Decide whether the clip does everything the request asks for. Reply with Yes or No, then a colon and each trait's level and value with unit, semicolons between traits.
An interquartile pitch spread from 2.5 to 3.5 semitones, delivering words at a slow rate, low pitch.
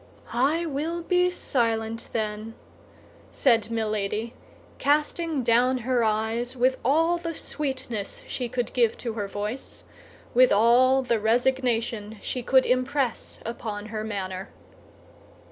No: average, 3.2 semitones; slow, 120 wpm; high, 240 Hz